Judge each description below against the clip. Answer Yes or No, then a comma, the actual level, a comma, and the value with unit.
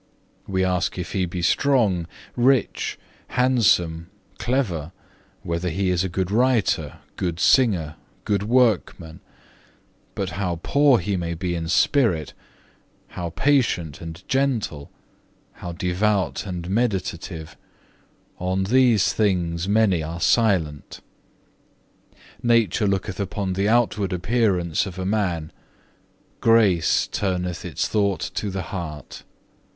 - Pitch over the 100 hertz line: No, very low, 95 Hz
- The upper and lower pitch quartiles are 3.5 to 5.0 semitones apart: Yes, average, 4.2 semitones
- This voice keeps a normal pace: No, slow, 115 wpm